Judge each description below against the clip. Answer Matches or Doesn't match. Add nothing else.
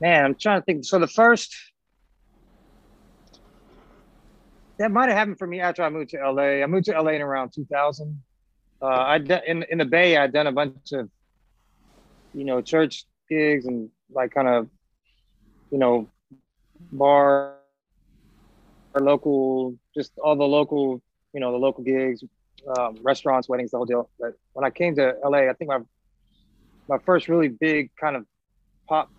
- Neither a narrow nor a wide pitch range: Matches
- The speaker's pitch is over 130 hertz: Matches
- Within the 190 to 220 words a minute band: Doesn't match